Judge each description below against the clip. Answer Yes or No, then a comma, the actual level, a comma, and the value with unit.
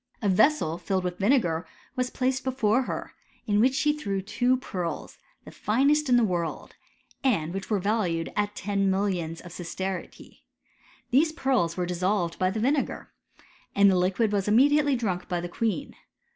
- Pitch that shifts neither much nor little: No, wide, 5.8 semitones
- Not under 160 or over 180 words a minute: Yes, average, 170 wpm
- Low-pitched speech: No, high, 205 Hz